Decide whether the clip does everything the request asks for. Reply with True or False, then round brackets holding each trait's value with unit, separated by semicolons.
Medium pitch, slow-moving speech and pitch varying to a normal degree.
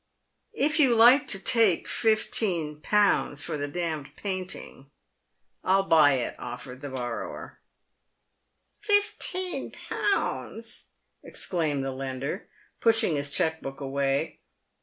False (165 Hz; 115 wpm; 8.2 semitones)